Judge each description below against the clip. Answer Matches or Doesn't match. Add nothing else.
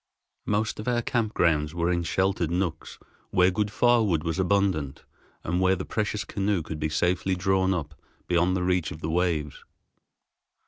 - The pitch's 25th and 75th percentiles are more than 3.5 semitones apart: Doesn't match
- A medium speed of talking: Matches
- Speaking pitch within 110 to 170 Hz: Doesn't match